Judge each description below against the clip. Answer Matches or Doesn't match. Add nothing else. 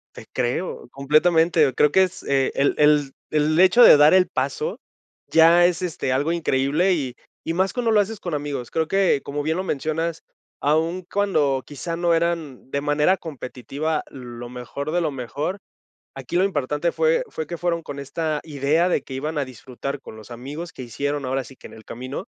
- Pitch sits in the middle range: Matches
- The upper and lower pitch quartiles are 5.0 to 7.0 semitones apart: Doesn't match